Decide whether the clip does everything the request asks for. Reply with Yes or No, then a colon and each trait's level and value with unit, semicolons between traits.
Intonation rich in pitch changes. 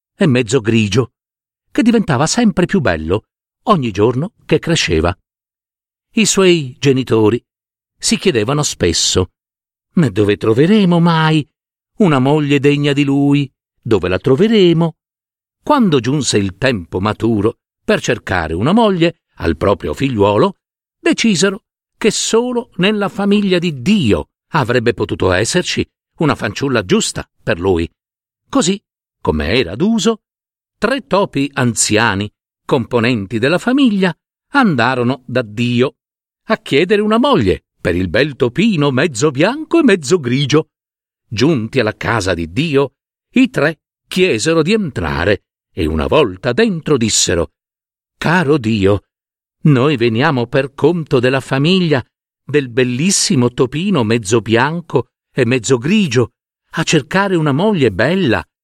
Yes: wide, 8.0 semitones